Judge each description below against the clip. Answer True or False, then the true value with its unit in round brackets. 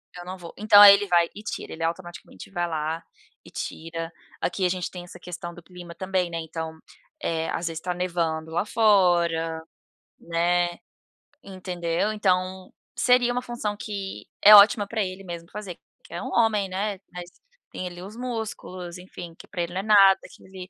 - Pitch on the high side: False (180 Hz)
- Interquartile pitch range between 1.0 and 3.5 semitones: True (2.8 semitones)